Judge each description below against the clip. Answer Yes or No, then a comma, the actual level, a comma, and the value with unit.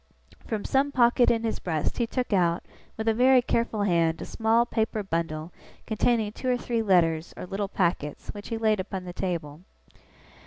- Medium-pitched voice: No, high, 210 Hz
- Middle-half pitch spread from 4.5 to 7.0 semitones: Yes, average, 5.1 semitones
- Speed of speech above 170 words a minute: Yes, average, 185 wpm